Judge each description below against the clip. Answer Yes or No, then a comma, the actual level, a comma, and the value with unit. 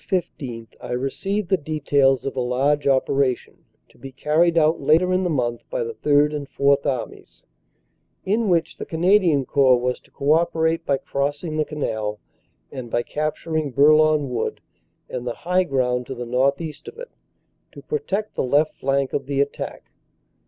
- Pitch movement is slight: No, average, 3.8 semitones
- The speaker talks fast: No, average, 170 wpm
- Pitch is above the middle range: No, medium, 145 Hz